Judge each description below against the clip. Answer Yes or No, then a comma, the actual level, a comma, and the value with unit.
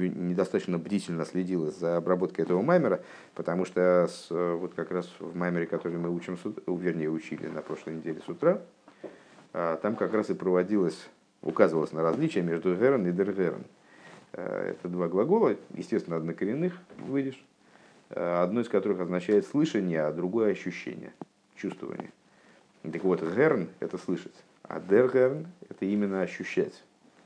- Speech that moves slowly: No, average, 135 wpm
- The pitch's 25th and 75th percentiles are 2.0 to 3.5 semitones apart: Yes, average, 3.1 semitones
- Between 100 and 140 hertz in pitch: No, very low, 90 Hz